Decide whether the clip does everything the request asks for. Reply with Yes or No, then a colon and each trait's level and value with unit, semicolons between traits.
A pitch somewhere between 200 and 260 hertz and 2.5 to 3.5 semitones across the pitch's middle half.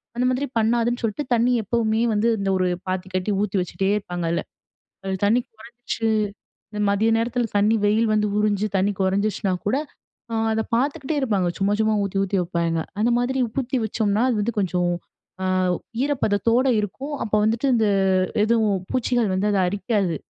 Yes: high, 215 Hz; average, 3.2 semitones